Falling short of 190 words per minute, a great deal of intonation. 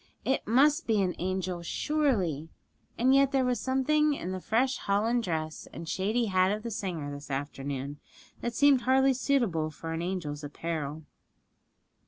Yes: average, 160 wpm; wide, 8.2 semitones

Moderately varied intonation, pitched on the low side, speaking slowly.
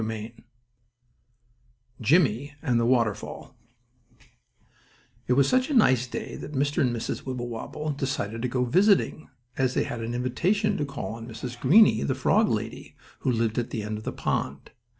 No: average, 4.0 semitones; low, 125 Hz; average, 170 wpm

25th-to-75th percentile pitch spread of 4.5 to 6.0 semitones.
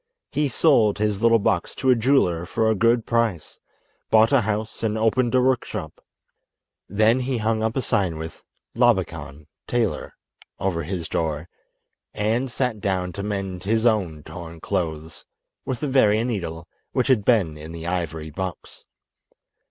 Yes: average, 5.2 semitones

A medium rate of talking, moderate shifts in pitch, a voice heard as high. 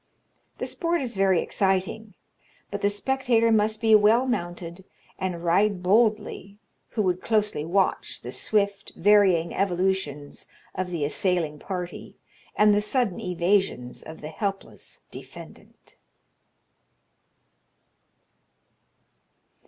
No: slow, 105 wpm; average, 3.2 semitones; high, 195 Hz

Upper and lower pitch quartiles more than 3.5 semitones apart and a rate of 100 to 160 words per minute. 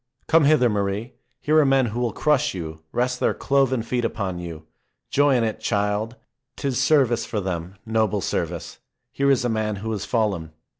No: average, 4.5 semitones; average, 185 wpm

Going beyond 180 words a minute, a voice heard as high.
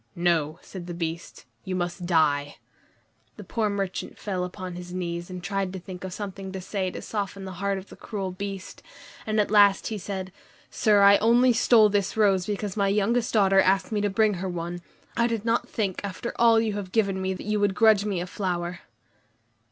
Yes: fast, 205 wpm; high, 195 Hz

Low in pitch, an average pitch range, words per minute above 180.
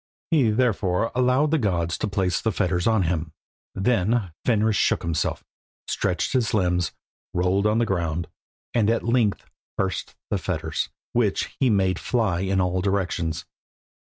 No: low, 100 Hz; average, 4.3 semitones; average, 150 wpm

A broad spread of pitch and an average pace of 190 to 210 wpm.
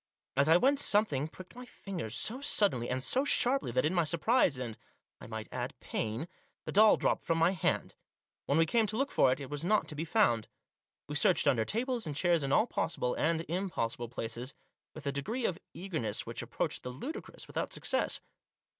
Yes: wide, 8.7 semitones; average, 200 wpm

